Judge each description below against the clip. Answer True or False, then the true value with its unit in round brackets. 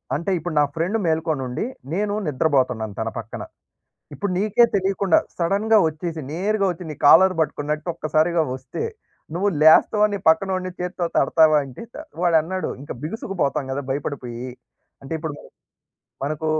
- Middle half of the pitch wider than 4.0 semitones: True (4.4 semitones)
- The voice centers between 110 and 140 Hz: False (160 Hz)